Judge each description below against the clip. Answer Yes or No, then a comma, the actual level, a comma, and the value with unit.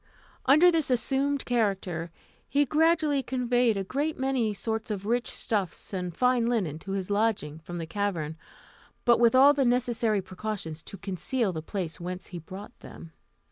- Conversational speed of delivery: Yes, average, 165 wpm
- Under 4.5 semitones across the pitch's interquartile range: No, wide, 5.6 semitones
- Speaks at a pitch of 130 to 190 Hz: No, high, 220 Hz